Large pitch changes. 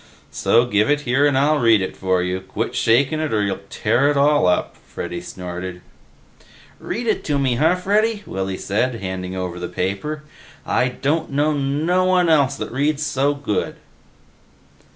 Yes: wide, 7.8 semitones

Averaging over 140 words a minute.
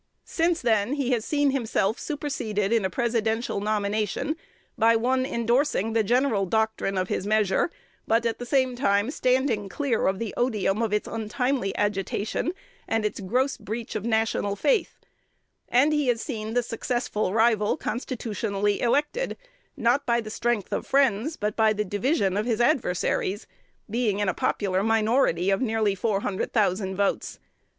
Yes: average, 160 wpm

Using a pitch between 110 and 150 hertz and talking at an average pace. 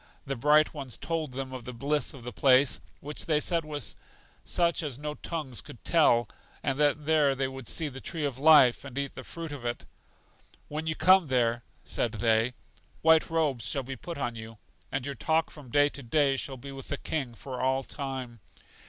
No: medium, 140 Hz; fast, 210 wpm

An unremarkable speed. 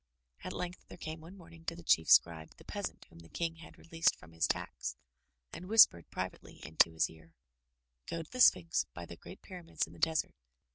No: fast, 210 wpm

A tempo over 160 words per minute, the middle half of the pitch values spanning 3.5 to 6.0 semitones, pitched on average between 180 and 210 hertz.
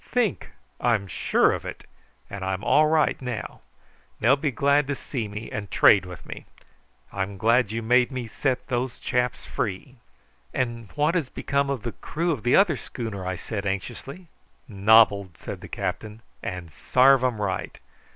No: average, 170 wpm; average, 5.3 semitones; low, 115 Hz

